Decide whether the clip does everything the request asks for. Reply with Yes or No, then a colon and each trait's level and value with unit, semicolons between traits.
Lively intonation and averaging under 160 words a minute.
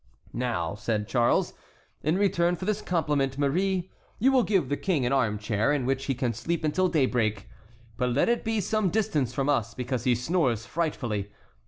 No: wide, 6.9 semitones; average, 180 wpm